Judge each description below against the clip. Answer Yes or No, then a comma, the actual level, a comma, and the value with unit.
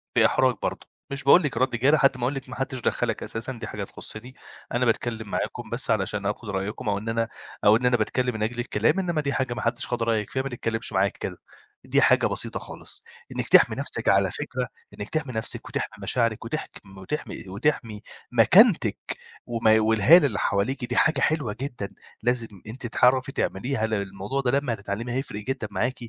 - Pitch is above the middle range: No, low, 120 Hz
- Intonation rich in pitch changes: No, average, 3.4 semitones